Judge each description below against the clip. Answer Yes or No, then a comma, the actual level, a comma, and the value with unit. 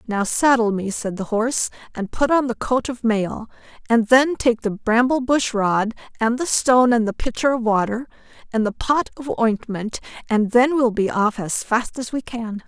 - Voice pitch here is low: No, high, 230 Hz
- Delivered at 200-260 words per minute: Yes, fast, 205 wpm